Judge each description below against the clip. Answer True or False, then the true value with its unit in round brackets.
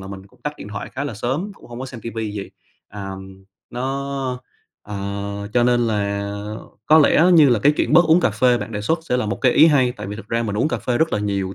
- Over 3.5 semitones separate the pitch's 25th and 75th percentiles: True (4.9 semitones)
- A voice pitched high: False (115 Hz)